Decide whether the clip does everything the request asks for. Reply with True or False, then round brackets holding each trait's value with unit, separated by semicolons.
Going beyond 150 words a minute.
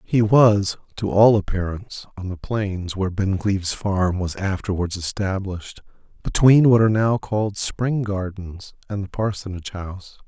False (145 wpm)